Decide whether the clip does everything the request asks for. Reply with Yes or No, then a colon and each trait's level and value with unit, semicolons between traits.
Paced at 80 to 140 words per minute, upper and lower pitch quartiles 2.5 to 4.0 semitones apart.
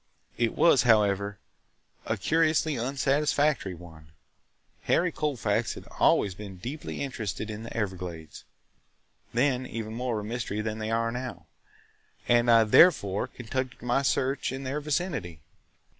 No: slow, 135 wpm; average, 4.7 semitones